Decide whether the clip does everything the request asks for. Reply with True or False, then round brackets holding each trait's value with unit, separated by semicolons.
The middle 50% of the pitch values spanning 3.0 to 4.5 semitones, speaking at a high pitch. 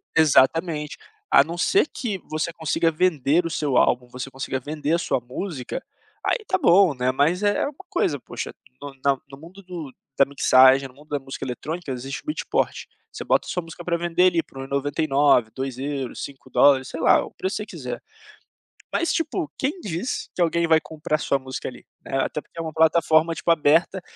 False (4.1 semitones; 155 Hz)